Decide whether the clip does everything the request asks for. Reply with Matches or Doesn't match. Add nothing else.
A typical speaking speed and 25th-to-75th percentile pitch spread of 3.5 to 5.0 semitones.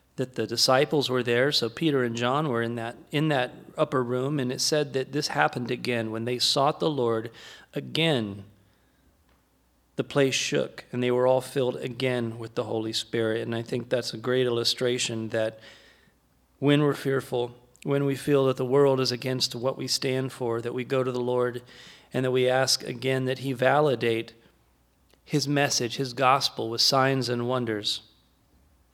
Doesn't match